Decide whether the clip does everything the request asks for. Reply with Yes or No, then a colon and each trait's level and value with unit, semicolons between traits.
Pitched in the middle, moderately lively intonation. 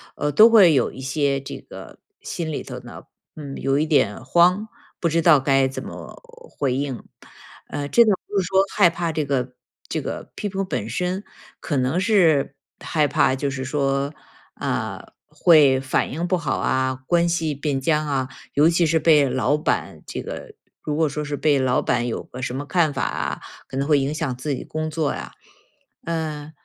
Yes: medium, 150 Hz; average, 3.6 semitones